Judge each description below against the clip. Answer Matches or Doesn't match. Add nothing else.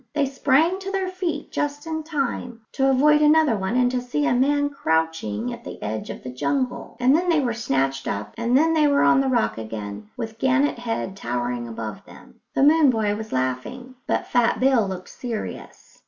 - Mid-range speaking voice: Doesn't match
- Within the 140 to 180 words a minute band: Doesn't match